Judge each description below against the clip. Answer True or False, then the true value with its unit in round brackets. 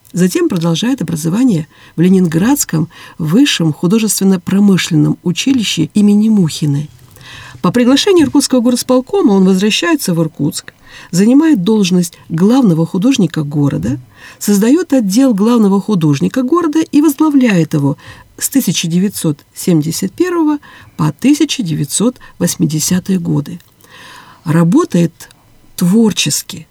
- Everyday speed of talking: False (85 wpm)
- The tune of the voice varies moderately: False (7.7 semitones)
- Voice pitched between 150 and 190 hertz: True (185 Hz)